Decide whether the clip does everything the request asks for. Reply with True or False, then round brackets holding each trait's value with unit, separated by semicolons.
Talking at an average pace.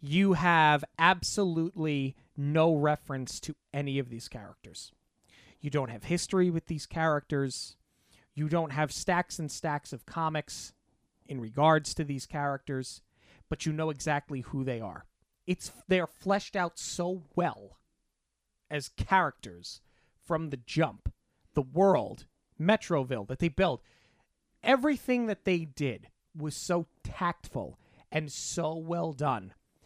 False (130 wpm)